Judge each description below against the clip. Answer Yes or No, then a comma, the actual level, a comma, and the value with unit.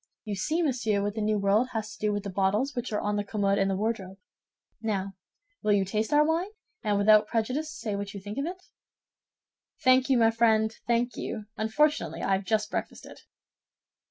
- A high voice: Yes, high, 215 Hz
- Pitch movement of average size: Yes, average, 3.0 semitones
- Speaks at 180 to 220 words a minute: Yes, average, 200 wpm